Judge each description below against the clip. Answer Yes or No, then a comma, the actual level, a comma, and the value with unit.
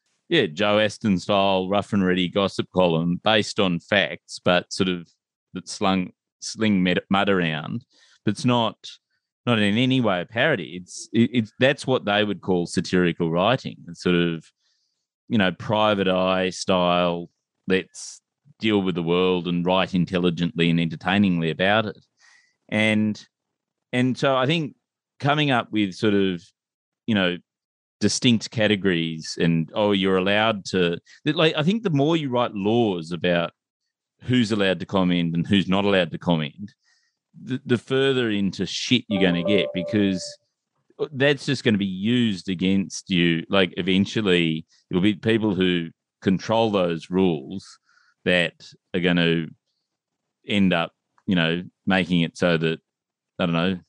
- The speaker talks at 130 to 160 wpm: Yes, average, 155 wpm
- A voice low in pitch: Yes, very low, 95 Hz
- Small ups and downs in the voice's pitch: No, average, 3.6 semitones